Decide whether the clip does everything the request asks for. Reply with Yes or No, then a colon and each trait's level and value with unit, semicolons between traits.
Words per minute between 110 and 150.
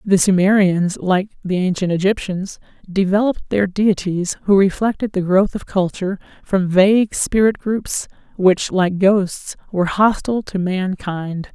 Yes: slow, 135 wpm